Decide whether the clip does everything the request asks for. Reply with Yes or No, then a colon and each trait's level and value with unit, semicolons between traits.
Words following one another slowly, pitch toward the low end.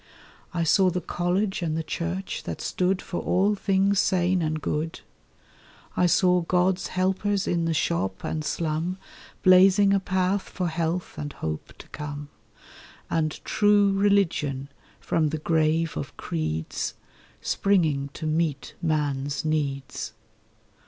No: slow, 130 wpm; medium, 170 Hz